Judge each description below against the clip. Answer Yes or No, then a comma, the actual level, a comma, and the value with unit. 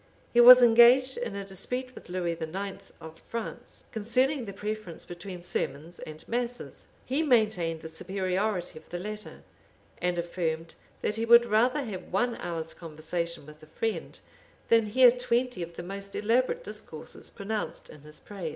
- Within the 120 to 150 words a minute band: No, average, 160 wpm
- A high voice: Yes, high, 200 Hz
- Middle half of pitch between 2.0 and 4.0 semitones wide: No, wide, 5.6 semitones